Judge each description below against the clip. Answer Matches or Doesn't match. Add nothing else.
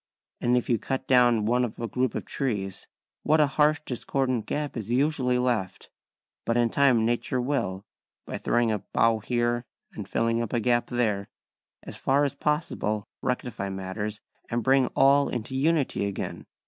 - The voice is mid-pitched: Doesn't match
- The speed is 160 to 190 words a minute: Matches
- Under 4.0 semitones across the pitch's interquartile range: Matches